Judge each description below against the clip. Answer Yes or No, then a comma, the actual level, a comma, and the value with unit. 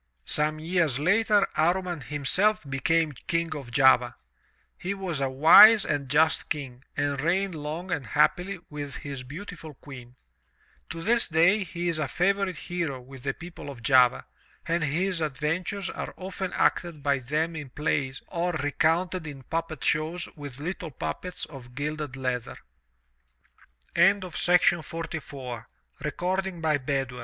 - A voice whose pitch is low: No, medium, 155 Hz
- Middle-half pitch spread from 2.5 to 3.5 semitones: No, average, 4.3 semitones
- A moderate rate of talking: No, slow, 130 wpm